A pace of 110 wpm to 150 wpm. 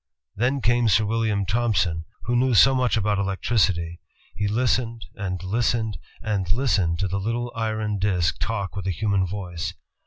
No: average, 165 wpm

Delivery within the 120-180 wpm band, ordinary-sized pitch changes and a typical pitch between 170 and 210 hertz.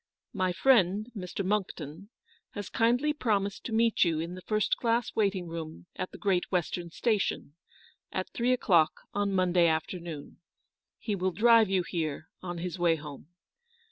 Yes: average, 165 wpm; average, 3.8 semitones; medium, 185 Hz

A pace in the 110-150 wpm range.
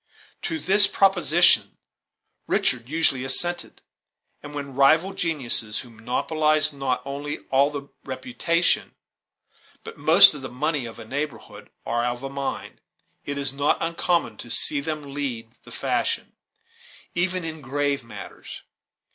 Yes: slow, 135 wpm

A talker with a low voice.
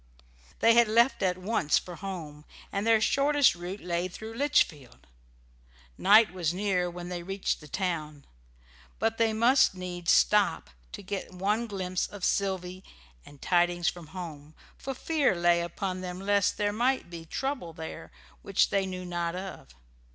No: medium, 185 Hz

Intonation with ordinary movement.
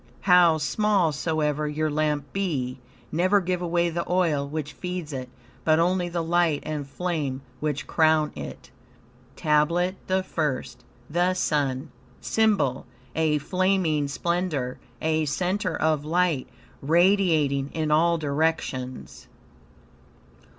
Yes: average, 3.3 semitones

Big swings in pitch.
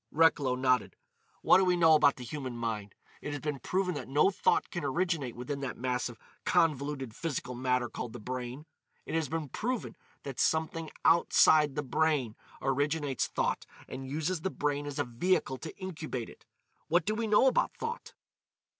No: average, 4.3 semitones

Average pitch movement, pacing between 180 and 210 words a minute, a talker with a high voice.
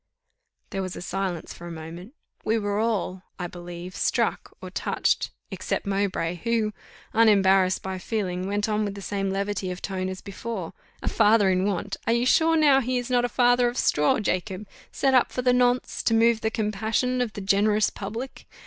Yes: average, 3.7 semitones; average, 195 wpm; high, 205 Hz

